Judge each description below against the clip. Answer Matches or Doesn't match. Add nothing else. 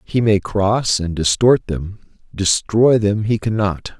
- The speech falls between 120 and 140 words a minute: Matches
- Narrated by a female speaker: Doesn't match